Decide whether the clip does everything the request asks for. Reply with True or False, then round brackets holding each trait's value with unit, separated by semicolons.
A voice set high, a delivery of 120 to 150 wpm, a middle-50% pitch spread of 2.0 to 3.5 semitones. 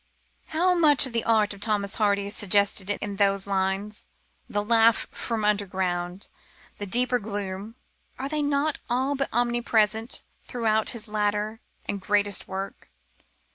True (210 Hz; 140 wpm; 2.9 semitones)